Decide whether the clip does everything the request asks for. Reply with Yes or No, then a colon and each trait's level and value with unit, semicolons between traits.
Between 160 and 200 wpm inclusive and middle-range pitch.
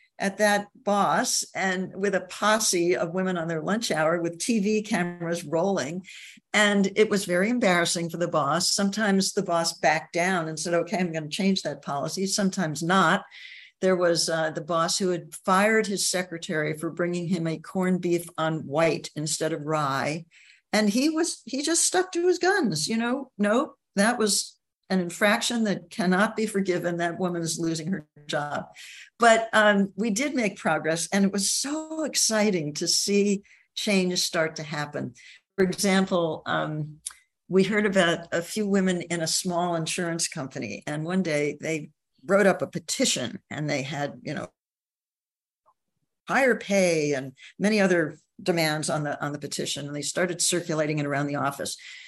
Yes: average, 175 wpm; medium, 180 Hz